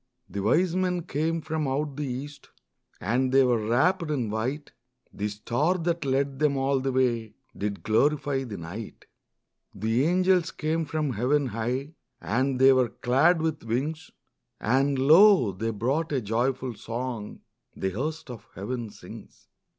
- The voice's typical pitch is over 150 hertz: No, low, 135 Hz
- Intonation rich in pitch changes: No, average, 4.7 semitones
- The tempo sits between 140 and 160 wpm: Yes, average, 150 wpm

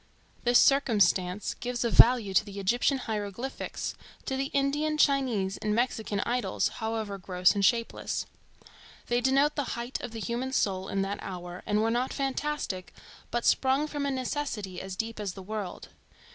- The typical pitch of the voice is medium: No, high, 230 Hz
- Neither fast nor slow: Yes, average, 165 wpm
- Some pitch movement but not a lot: Yes, average, 4.9 semitones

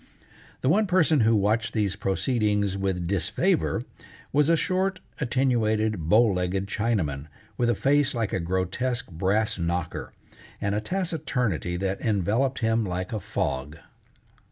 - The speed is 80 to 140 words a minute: Yes, slow, 135 wpm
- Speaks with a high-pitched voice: No, low, 110 Hz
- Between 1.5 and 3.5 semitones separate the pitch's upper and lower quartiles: No, average, 5.1 semitones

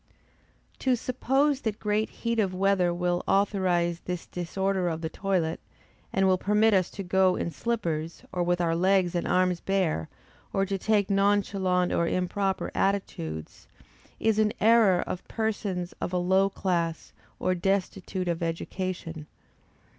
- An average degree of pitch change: No, narrow, 2.3 semitones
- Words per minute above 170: No, average, 145 wpm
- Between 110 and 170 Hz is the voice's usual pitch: No, medium, 185 Hz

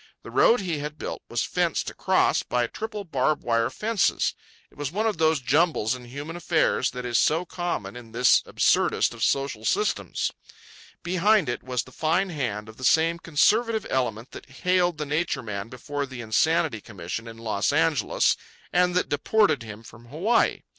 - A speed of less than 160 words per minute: No, average, 175 wpm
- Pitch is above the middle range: No, medium, 145 Hz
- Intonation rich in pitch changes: Yes, wide, 6.7 semitones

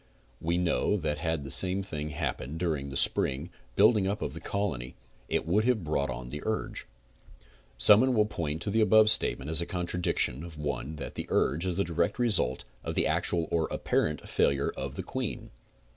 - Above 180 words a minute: Yes, average, 200 wpm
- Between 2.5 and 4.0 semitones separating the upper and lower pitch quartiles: No, average, 5.1 semitones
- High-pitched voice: No, very low, 85 Hz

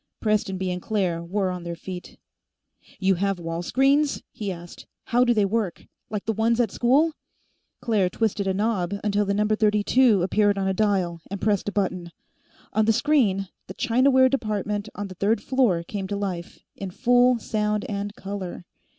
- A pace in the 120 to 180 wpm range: Yes, average, 175 wpm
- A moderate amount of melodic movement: Yes, average, 3.0 semitones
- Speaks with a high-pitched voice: Yes, high, 205 Hz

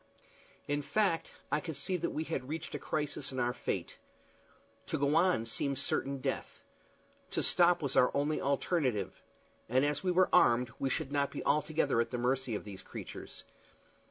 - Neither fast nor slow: Yes, average, 180 wpm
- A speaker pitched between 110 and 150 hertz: Yes, medium, 140 Hz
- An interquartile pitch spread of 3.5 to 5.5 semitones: Yes, average, 4.0 semitones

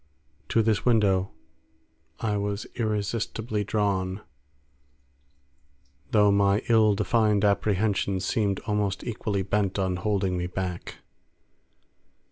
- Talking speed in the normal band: No, slow, 95 wpm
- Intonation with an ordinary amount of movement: No, narrow, 1.9 semitones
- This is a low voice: Yes, low, 100 Hz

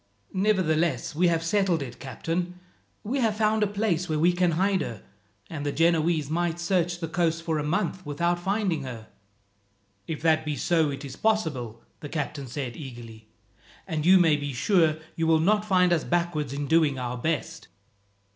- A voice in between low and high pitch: Yes, medium, 165 Hz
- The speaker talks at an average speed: Yes, average, 180 wpm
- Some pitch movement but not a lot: Yes, average, 3.6 semitones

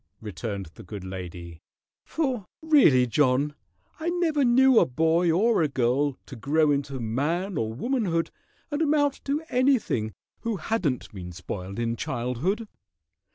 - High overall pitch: No, medium, 150 Hz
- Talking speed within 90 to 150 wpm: Yes, average, 140 wpm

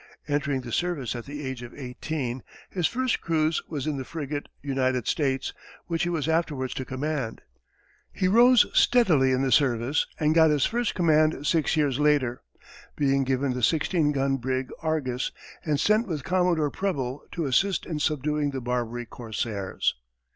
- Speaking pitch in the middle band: Yes, medium, 145 Hz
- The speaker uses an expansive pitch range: No, average, 3.6 semitones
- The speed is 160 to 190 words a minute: Yes, average, 165 wpm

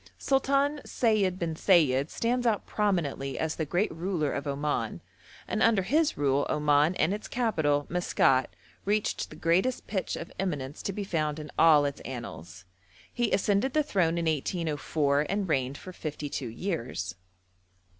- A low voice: No, medium, 165 Hz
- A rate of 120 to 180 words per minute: Yes, average, 155 wpm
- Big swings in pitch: Yes, wide, 5.8 semitones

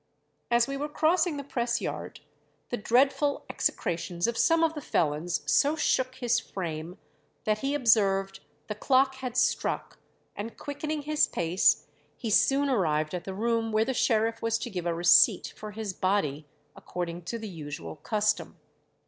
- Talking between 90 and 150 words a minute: No, average, 165 wpm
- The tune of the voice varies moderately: No, wide, 6.8 semitones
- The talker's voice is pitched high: Yes, high, 225 Hz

